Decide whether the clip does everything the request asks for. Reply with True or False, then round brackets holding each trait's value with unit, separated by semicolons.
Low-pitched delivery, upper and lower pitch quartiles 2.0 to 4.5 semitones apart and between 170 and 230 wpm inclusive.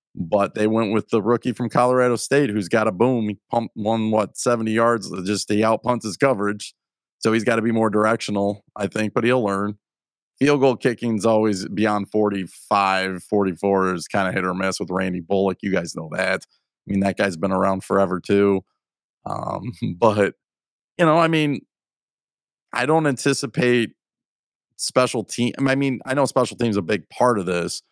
True (110 Hz; 3.7 semitones; 185 wpm)